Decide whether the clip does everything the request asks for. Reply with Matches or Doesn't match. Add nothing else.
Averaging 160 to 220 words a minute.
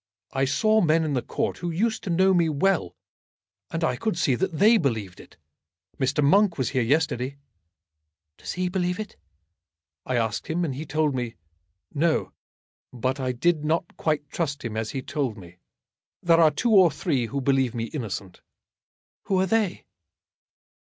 Matches